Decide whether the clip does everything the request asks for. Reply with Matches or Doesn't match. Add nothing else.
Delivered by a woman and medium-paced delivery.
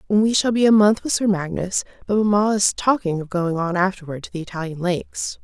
Doesn't match